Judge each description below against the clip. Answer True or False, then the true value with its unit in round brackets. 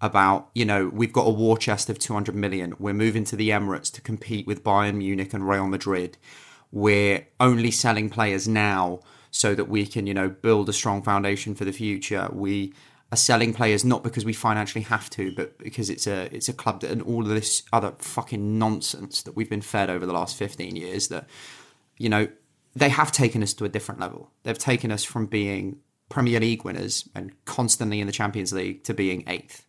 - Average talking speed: False (210 wpm)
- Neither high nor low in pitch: False (105 Hz)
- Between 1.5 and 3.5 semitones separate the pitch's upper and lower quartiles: True (2.4 semitones)